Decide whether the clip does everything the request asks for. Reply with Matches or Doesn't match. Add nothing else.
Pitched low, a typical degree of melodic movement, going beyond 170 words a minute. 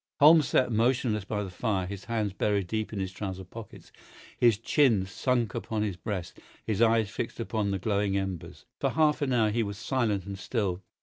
Matches